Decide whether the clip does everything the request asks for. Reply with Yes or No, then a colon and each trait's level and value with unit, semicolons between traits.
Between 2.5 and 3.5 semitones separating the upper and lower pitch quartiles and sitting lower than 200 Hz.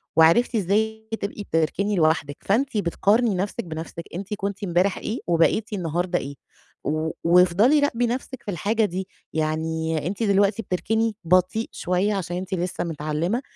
No: average, 4.4 semitones; medium, 185 Hz